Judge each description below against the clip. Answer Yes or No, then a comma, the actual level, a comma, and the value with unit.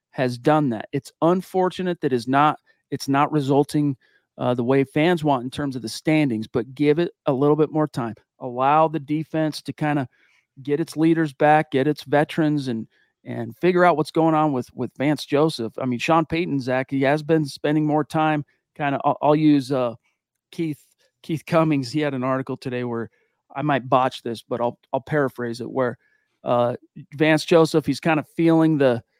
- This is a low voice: No, medium, 145 Hz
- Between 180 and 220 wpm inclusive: Yes, average, 200 wpm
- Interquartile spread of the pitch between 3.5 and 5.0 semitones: No, average, 3.0 semitones